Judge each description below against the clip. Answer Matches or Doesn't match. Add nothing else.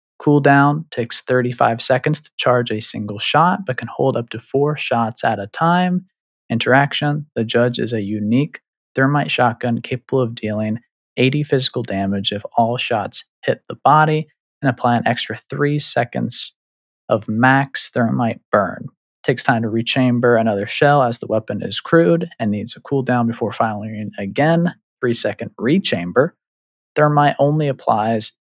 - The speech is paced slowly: Doesn't match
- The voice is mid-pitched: Doesn't match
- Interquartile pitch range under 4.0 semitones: Doesn't match